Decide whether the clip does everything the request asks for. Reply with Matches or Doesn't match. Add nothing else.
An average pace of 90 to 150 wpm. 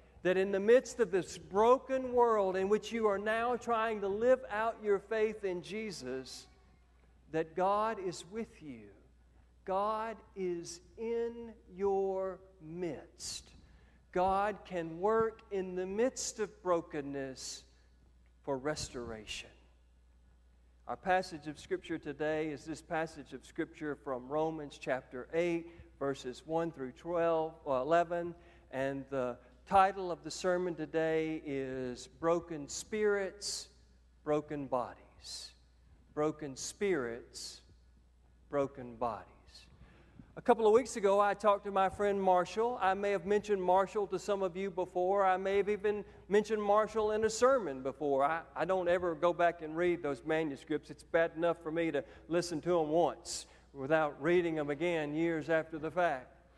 Matches